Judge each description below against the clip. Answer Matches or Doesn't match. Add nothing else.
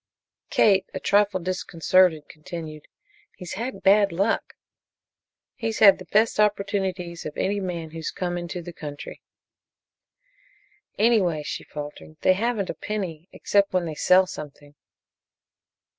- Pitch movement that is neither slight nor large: Matches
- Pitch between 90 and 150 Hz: Doesn't match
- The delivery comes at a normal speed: Doesn't match